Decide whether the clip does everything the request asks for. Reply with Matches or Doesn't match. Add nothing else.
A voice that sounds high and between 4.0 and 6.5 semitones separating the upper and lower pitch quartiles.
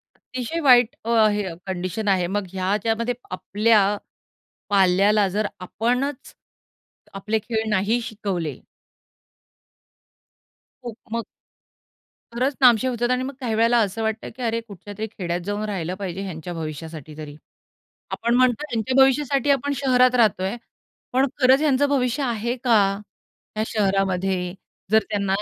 Matches